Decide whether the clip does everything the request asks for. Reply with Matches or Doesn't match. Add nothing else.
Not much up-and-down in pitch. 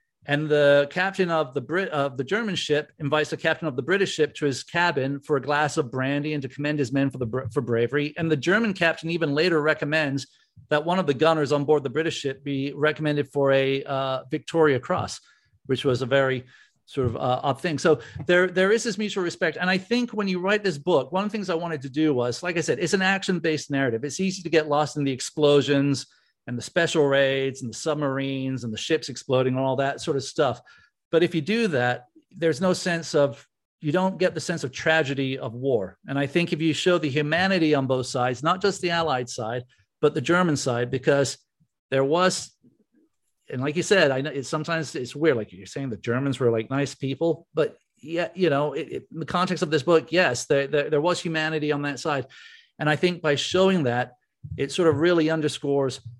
Doesn't match